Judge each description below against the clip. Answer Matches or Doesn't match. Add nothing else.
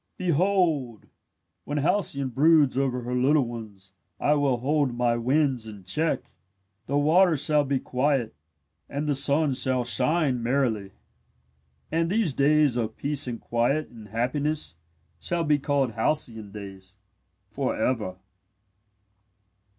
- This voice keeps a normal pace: Doesn't match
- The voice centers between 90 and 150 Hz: Matches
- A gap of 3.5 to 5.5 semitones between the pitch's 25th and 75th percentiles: Matches